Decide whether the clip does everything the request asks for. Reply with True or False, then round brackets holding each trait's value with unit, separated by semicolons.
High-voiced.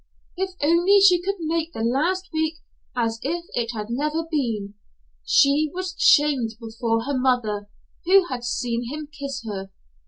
True (285 Hz)